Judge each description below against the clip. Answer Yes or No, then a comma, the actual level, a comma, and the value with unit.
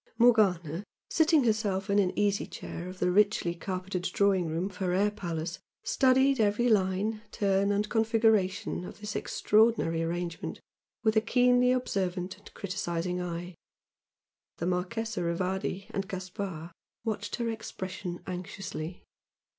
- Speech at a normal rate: No, slow, 130 wpm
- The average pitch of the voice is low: No, high, 195 Hz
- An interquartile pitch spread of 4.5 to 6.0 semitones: No, average, 3.2 semitones